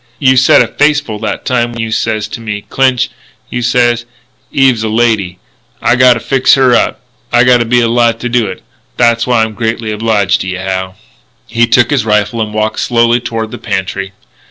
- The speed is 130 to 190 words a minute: No, fast, 205 wpm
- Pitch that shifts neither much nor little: No, narrow, 2.2 semitones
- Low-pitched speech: Yes, low, 115 Hz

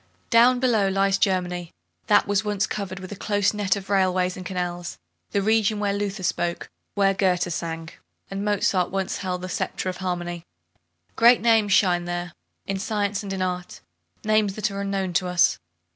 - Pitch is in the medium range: No, high, 195 Hz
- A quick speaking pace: No, average, 175 wpm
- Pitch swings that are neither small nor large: No, narrow, 2.2 semitones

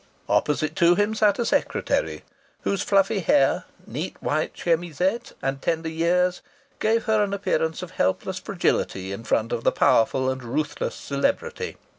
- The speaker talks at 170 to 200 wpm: No, average, 150 wpm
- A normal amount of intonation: No, wide, 6.7 semitones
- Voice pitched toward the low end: No, medium, 170 Hz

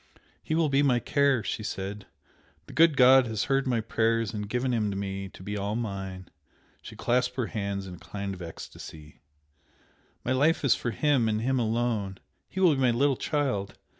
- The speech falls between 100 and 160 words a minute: No, average, 195 wpm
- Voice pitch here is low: Yes, low, 115 Hz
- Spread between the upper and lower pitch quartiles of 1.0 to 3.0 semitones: No, average, 4.9 semitones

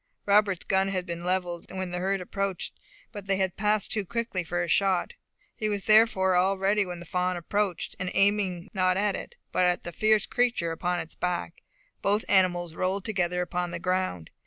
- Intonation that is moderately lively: No, narrow, 2.1 semitones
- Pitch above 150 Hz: Yes, medium, 185 Hz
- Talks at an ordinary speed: Yes, average, 190 wpm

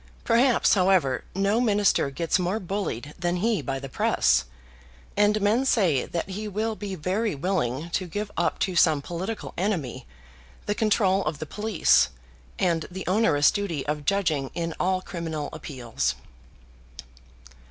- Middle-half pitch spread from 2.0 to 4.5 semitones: No, average, 5.3 semitones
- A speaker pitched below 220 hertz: Yes, medium, 185 Hz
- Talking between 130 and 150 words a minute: Yes, average, 145 wpm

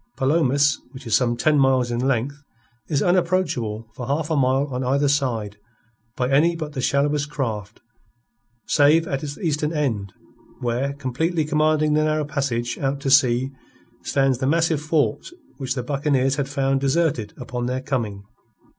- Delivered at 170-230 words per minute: No, average, 160 wpm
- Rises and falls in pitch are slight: No, average, 3.0 semitones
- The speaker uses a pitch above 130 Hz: Yes, medium, 140 Hz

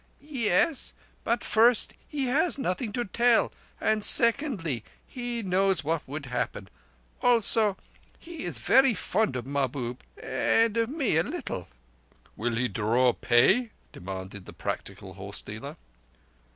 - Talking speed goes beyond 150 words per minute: No, slow, 135 wpm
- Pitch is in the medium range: No, high, 205 Hz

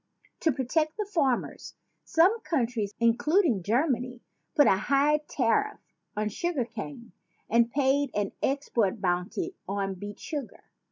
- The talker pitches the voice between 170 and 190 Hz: No, very high, 250 Hz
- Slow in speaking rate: Yes, slow, 125 wpm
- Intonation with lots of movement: Yes, wide, 6.2 semitones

